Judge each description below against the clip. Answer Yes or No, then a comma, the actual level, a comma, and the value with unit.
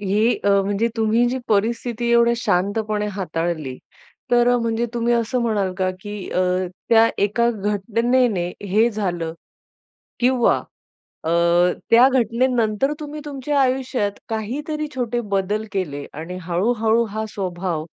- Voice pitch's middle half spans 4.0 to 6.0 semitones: No, average, 3.5 semitones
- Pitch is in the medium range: No, high, 220 Hz